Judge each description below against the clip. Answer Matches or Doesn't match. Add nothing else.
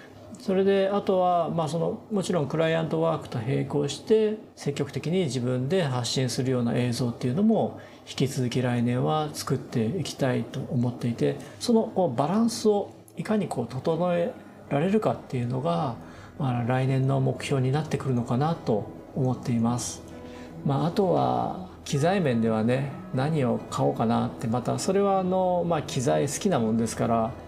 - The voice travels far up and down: Matches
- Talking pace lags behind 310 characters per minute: Doesn't match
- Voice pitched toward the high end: Doesn't match